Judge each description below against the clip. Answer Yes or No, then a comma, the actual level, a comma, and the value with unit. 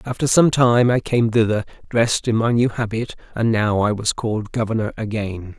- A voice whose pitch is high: No, low, 115 Hz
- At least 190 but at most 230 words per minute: Yes, average, 195 wpm